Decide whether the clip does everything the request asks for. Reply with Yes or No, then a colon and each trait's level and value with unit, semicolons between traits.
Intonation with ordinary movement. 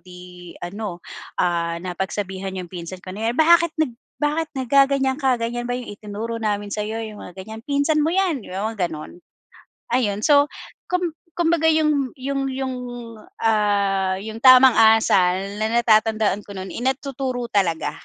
No: wide, 5.8 semitones